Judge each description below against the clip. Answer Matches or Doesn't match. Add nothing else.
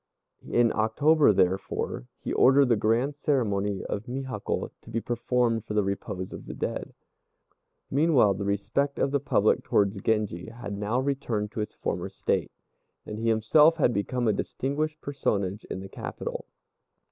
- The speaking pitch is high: Doesn't match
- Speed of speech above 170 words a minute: Doesn't match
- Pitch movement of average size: Matches